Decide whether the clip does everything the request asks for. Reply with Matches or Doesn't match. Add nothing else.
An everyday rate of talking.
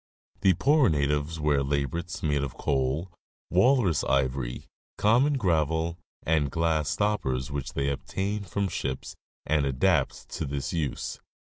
Doesn't match